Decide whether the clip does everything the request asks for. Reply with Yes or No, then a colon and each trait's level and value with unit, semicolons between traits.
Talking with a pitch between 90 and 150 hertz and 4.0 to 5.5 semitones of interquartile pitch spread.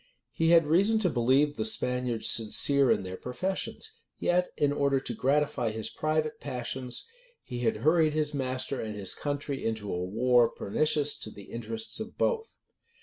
Yes: low, 135 Hz; average, 4.9 semitones